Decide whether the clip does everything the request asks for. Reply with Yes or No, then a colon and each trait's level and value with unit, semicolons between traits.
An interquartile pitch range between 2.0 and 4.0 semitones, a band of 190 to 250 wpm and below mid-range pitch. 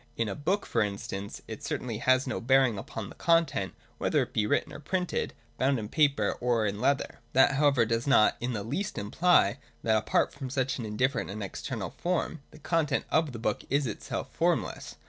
No: average, 4.9 semitones; average, 200 wpm; low, 130 Hz